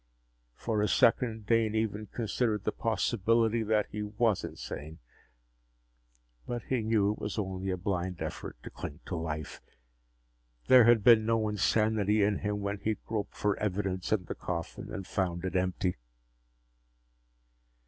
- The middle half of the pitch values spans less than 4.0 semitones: Yes, average, 2.8 semitones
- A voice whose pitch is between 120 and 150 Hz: No, low, 105 Hz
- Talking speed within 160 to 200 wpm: No, average, 150 wpm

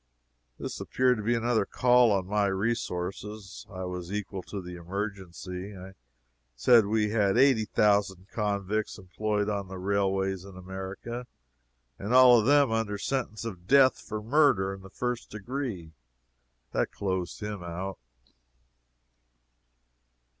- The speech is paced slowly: Yes, slow, 130 wpm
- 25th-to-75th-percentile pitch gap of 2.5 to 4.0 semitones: Yes, average, 3.1 semitones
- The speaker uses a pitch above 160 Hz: No, low, 100 Hz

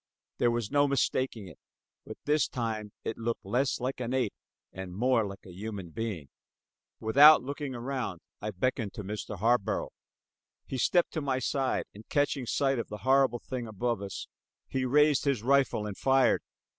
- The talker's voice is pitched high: No, low, 120 Hz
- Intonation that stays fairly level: No, average, 4.2 semitones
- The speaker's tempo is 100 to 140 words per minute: No, average, 170 wpm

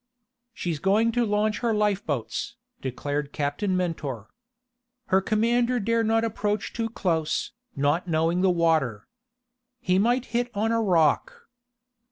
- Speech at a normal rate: No, slow, 130 wpm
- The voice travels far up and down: Yes, wide, 6.1 semitones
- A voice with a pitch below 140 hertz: No, high, 195 Hz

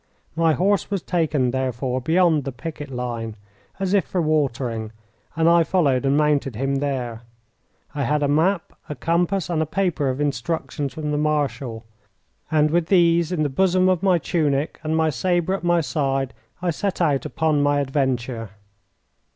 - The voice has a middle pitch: Yes, medium, 150 Hz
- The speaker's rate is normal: Yes, average, 170 wpm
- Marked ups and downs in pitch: No, average, 4.0 semitones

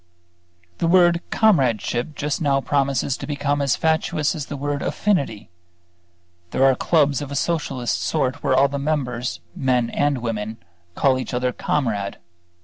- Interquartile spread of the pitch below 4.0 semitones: Yes, average, 2.9 semitones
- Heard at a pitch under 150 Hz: Yes, medium, 140 Hz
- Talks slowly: No, average, 150 wpm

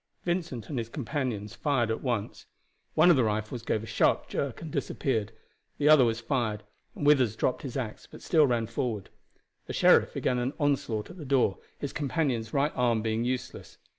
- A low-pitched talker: Yes, low, 125 Hz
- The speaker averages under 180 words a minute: No, average, 190 wpm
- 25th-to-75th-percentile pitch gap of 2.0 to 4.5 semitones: Yes, average, 4.1 semitones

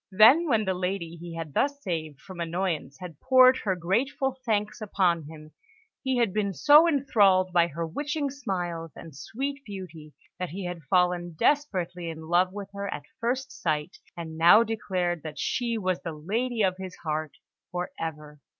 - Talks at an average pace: Yes, average, 175 wpm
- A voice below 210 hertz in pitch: Yes, medium, 185 Hz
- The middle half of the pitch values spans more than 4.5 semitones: Yes, average, 5.2 semitones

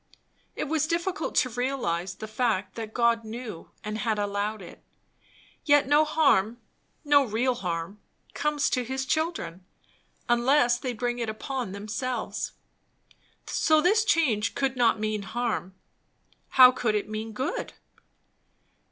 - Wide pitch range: No, average, 4.3 semitones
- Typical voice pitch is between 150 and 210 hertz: No, high, 240 Hz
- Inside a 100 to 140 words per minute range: Yes, slow, 135 wpm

